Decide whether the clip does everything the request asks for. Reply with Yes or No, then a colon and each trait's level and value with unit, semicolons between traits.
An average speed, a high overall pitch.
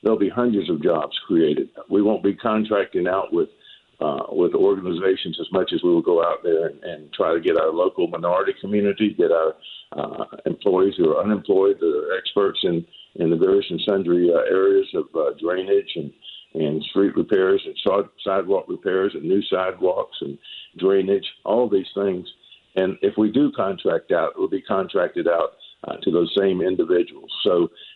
Yes: average, 185 wpm; very high, 390 Hz